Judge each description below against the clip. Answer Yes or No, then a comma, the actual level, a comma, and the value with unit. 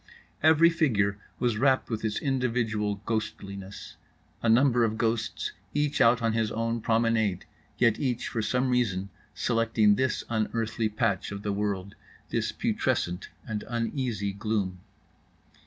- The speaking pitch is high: No, low, 110 Hz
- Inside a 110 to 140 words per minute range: Yes, slow, 135 wpm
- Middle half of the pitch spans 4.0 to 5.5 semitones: No, average, 2.8 semitones